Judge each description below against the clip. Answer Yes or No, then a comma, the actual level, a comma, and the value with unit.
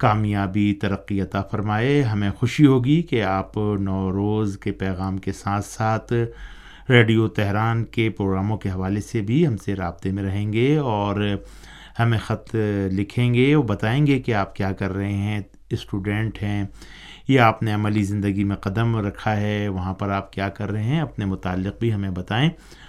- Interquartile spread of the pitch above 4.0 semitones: No, average, 2.7 semitones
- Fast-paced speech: No, average, 175 wpm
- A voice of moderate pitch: No, low, 105 Hz